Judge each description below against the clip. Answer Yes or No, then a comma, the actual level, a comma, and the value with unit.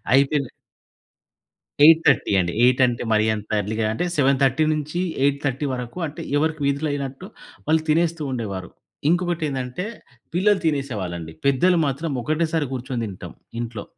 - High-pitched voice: No, medium, 140 Hz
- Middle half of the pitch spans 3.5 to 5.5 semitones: Yes, average, 4.5 semitones